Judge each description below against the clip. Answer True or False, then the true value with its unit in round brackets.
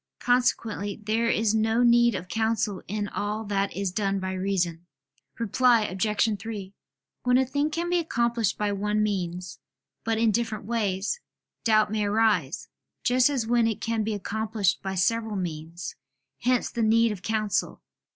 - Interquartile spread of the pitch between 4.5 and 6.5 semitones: False (2.7 semitones)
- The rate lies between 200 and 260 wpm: False (160 wpm)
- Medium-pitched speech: False (215 Hz)